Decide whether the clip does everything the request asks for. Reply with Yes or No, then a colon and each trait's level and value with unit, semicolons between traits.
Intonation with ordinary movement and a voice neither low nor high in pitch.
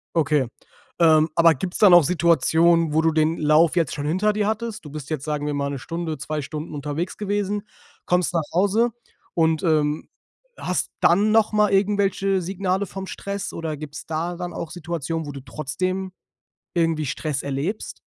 Yes: average, 3.8 semitones; medium, 165 Hz